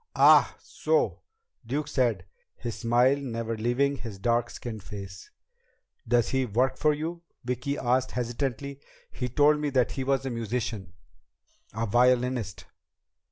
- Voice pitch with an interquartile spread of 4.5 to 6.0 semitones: No, average, 3.1 semitones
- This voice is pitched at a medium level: No, low, 125 Hz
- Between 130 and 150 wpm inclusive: Yes, average, 140 wpm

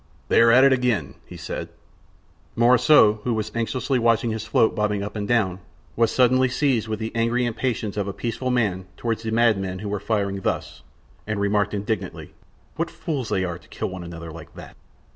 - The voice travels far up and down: No, average, 3.1 semitones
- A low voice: Yes, low, 110 Hz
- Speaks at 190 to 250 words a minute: Yes, average, 195 wpm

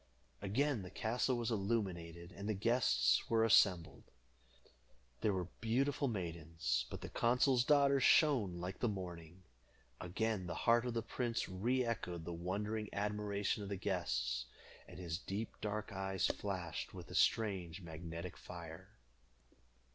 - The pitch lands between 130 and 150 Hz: No, low, 100 Hz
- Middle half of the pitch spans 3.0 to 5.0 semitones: Yes, average, 4.7 semitones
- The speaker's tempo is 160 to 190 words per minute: No, average, 140 wpm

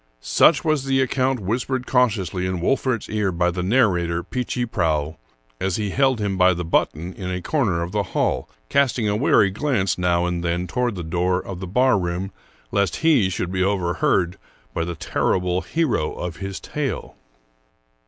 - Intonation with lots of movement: Yes, wide, 5.9 semitones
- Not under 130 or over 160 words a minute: No, average, 175 wpm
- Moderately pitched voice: No, very low, 95 Hz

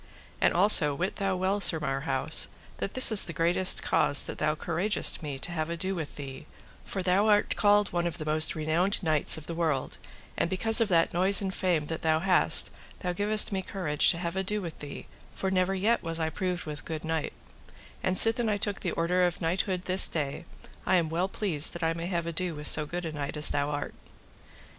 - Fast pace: Yes, fast, 220 wpm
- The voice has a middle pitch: Yes, medium, 175 Hz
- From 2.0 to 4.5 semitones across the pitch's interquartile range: Yes, average, 3.3 semitones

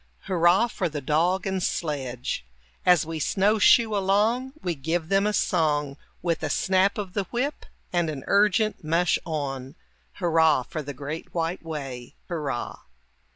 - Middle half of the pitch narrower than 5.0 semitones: Yes, average, 4.6 semitones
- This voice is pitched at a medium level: Yes, medium, 170 Hz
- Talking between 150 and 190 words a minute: Yes, average, 155 wpm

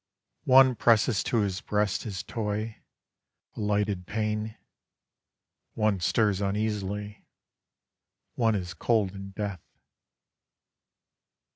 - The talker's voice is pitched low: Yes, low, 105 Hz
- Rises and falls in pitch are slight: Yes, narrow, 1.9 semitones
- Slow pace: Yes, slow, 95 wpm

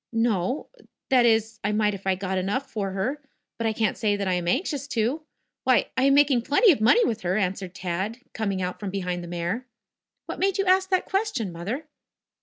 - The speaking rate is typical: No, fast, 210 wpm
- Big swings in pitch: Yes, wide, 5.9 semitones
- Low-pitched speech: No, high, 215 Hz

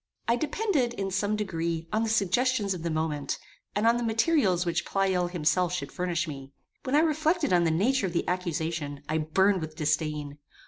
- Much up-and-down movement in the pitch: Yes, wide, 5.9 semitones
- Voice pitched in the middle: Yes, medium, 180 Hz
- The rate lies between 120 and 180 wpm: No, average, 190 wpm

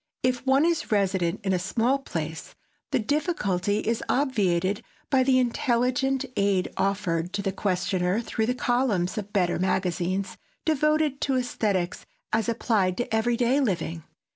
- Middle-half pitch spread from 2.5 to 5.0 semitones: No, wide, 5.4 semitones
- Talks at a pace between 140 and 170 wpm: Yes, average, 150 wpm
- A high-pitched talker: Yes, high, 215 Hz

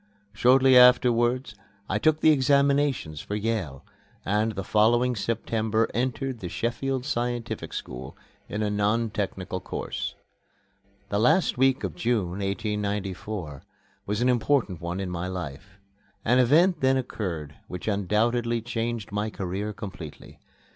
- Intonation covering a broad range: No, average, 4.2 semitones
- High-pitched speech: No, low, 110 Hz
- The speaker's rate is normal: No, slow, 130 wpm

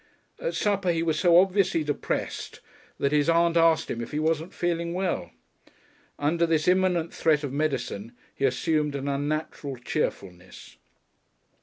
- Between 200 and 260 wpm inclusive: No, average, 145 wpm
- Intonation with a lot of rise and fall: No, average, 3.1 semitones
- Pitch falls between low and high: Yes, medium, 160 Hz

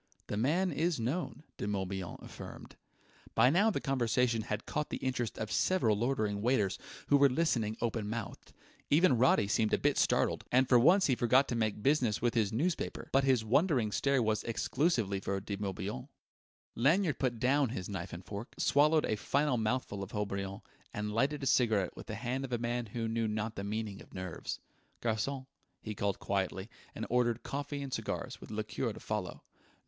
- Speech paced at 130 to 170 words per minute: No, average, 185 wpm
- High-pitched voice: No, low, 115 Hz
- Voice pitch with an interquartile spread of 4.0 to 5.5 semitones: Yes, average, 4.4 semitones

